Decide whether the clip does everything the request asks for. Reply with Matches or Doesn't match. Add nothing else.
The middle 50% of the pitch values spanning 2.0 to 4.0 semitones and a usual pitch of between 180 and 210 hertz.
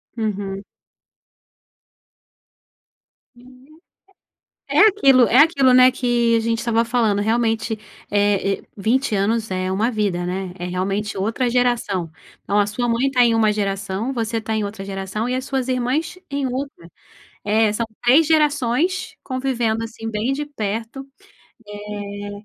Doesn't match